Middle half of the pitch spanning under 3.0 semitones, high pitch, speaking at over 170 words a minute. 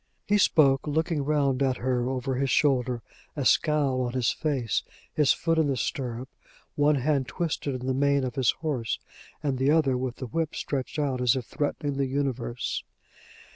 No: narrow, 2.6 semitones; low, 135 Hz; average, 180 wpm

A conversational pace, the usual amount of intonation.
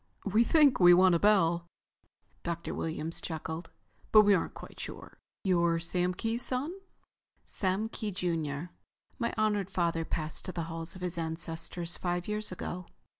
Yes: average, 155 wpm; average, 3.6 semitones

